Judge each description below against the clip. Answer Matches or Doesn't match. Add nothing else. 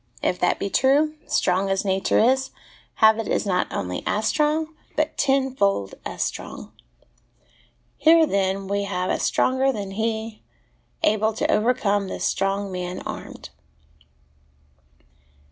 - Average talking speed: Doesn't match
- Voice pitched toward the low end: Doesn't match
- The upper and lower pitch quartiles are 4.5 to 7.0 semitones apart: Matches